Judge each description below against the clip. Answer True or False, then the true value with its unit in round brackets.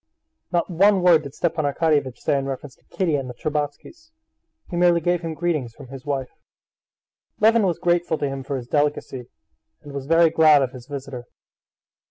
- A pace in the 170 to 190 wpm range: True (185 wpm)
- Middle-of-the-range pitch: True (150 Hz)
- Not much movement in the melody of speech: False (4.0 semitones)